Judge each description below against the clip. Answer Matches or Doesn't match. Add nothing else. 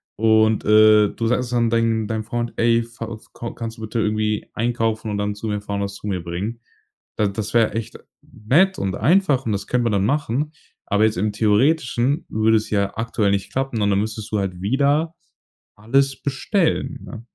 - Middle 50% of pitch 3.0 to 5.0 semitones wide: Doesn't match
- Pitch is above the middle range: Doesn't match